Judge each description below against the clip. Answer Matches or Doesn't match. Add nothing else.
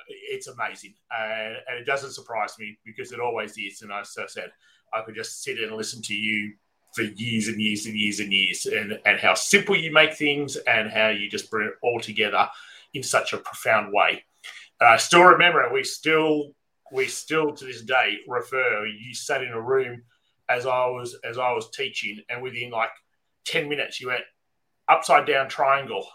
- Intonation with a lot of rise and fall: Matches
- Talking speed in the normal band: Matches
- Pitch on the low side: Matches